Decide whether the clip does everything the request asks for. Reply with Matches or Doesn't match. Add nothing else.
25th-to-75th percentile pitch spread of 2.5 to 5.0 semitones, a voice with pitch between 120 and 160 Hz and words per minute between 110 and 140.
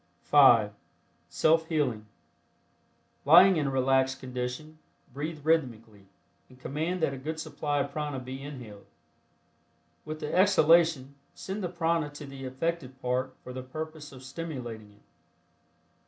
Matches